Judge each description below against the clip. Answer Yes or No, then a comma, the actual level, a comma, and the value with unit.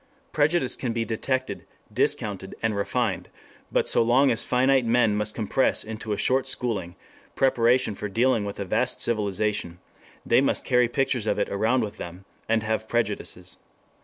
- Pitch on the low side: Yes, low, 115 Hz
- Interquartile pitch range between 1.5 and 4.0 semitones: Yes, average, 3.3 semitones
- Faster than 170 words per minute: No, average, 160 wpm